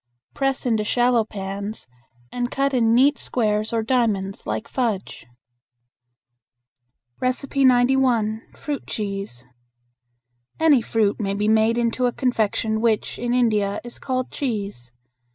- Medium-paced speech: No, slow, 115 wpm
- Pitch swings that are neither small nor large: Yes, average, 3.2 semitones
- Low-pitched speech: No, high, 230 Hz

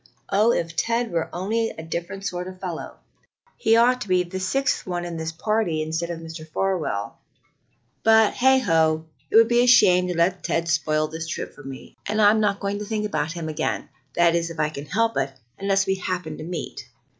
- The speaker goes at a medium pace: No, fast, 210 wpm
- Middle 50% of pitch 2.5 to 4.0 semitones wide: No, average, 4.5 semitones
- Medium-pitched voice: Yes, medium, 180 Hz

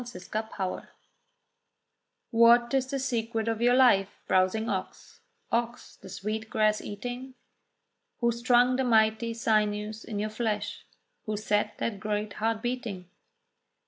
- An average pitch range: No, narrow, 2.3 semitones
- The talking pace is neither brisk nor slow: No, slow, 125 wpm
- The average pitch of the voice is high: Yes, high, 220 Hz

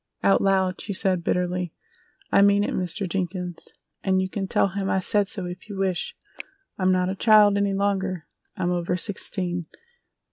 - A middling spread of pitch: No, narrow, 1.7 semitones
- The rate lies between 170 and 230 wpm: Yes, average, 175 wpm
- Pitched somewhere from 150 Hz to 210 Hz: Yes, high, 190 Hz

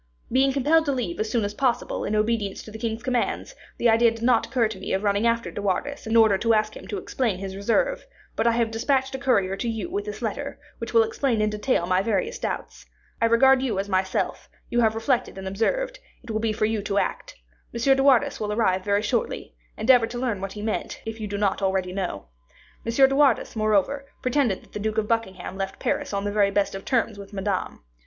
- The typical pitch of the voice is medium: No, high, 225 Hz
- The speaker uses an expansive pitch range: No, average, 3.8 semitones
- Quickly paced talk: Yes, fast, 235 wpm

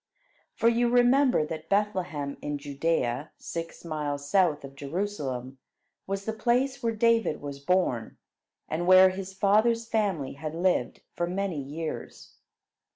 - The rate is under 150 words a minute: Yes, slow, 135 wpm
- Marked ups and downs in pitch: Yes, wide, 6.3 semitones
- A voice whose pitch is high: No, medium, 175 Hz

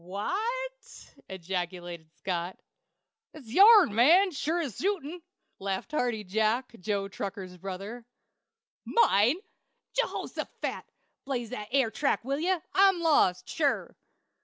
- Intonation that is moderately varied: No, wide, 8.3 semitones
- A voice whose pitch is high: Yes, high, 230 Hz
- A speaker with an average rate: No, slow, 110 wpm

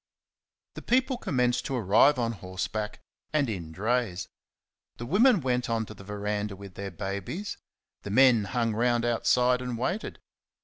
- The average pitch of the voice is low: Yes, low, 115 Hz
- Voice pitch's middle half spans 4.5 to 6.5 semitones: No, average, 3.8 semitones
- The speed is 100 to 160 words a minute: Yes, average, 150 wpm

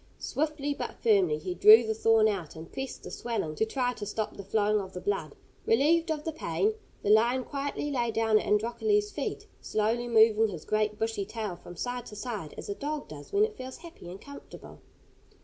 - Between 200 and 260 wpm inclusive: Yes, fast, 205 wpm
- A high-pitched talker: Yes, high, 225 Hz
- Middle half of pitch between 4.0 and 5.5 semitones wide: Yes, average, 4.7 semitones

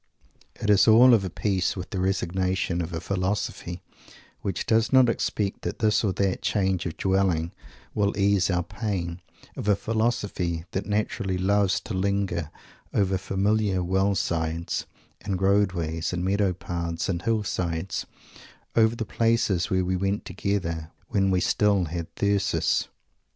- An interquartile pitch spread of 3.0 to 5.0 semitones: No, narrow, 2.6 semitones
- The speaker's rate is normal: Yes, average, 150 wpm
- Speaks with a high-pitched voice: No, very low, 95 Hz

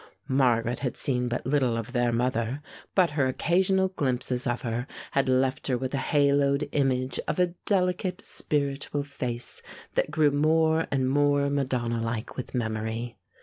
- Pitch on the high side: No, low, 135 Hz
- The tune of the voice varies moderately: Yes, average, 3.0 semitones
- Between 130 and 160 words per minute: Yes, average, 155 wpm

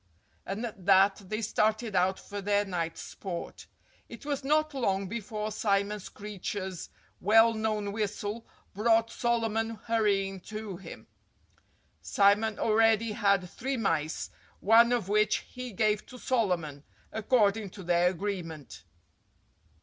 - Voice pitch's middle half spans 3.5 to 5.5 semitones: No, narrow, 2.5 semitones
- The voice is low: No, high, 210 Hz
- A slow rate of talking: Yes, slow, 125 wpm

